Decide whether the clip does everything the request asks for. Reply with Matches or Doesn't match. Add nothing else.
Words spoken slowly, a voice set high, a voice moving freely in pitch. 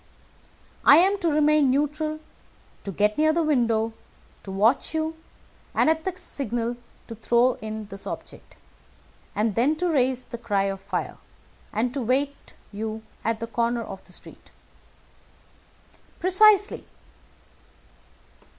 Matches